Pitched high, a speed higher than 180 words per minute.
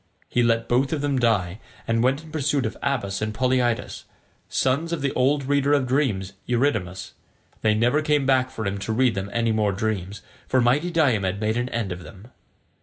No: low, 120 Hz; average, 195 wpm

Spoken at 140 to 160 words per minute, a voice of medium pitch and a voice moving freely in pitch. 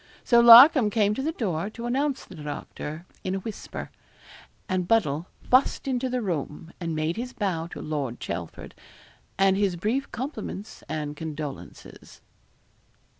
No: average, 145 wpm; high, 195 Hz; wide, 7.2 semitones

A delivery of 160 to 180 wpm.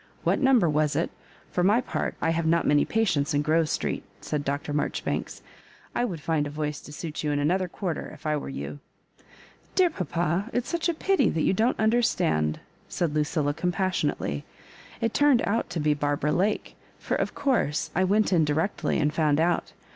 No: average, 200 wpm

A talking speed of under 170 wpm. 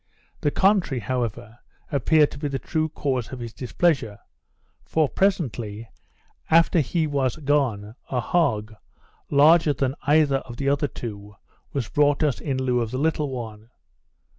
Yes: average, 150 wpm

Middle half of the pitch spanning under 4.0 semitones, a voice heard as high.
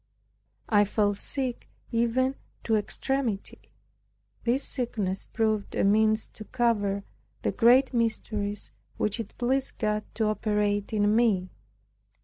Yes: narrow, 2.6 semitones; high, 220 Hz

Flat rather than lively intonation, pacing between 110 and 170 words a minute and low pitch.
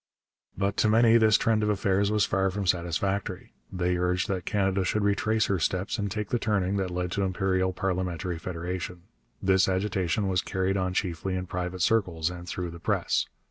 No: narrow, 1.9 semitones; average, 185 wpm; very low, 95 Hz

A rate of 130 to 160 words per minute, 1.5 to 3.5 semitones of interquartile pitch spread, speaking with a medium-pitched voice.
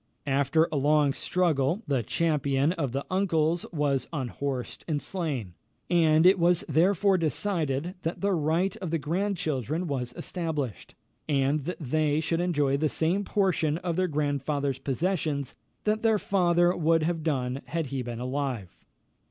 No: average, 150 wpm; average, 3.9 semitones; medium, 155 Hz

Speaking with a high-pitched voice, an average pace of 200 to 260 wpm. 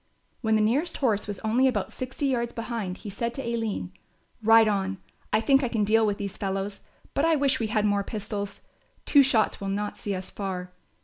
Yes: high, 220 Hz; fast, 205 wpm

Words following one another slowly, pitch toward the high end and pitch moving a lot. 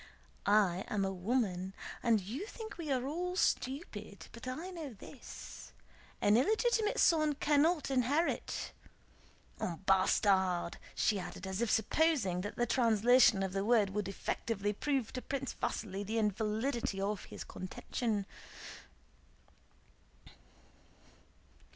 Yes: slow, 120 wpm; high, 225 Hz; wide, 6.0 semitones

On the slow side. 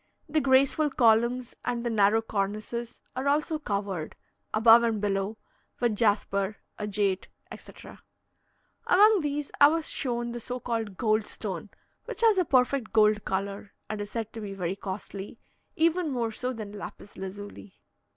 No: average, 150 wpm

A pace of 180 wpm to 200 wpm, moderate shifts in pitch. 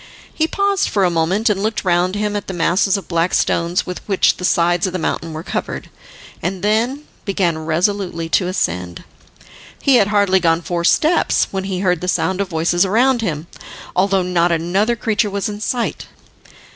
Yes: average, 185 wpm; average, 3.3 semitones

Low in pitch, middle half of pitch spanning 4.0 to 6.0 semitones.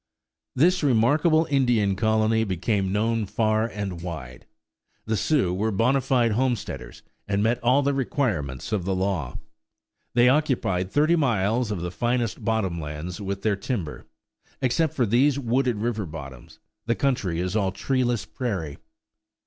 Yes: low, 110 Hz; average, 5.0 semitones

